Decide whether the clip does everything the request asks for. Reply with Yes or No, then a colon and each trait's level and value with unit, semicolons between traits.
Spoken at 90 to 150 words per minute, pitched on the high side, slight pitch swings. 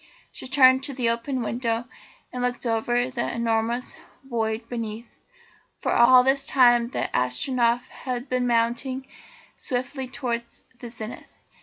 Yes: average, 140 wpm; high, 245 Hz; narrow, 1.7 semitones